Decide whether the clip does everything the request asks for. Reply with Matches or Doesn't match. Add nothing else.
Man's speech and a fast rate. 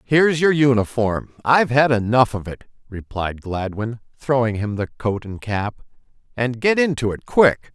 Doesn't match